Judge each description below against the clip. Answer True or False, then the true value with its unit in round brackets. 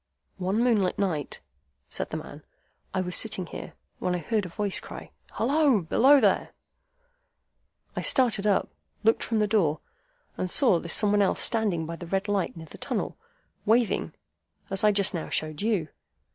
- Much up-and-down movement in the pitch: False (3.8 semitones)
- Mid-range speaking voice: False (200 Hz)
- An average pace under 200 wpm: True (175 wpm)